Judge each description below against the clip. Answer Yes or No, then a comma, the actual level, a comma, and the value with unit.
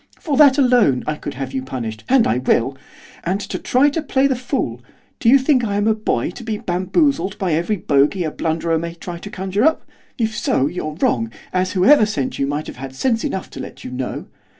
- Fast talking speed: Yes, fast, 220 wpm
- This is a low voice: No, medium, 185 Hz